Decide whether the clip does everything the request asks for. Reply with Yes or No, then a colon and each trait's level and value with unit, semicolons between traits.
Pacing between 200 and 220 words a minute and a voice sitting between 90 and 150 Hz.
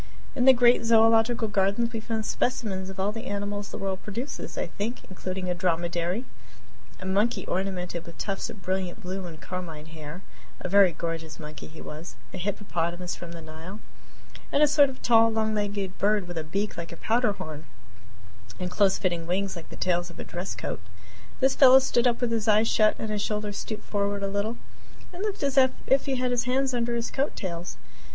No: fast, 205 wpm; high, 200 Hz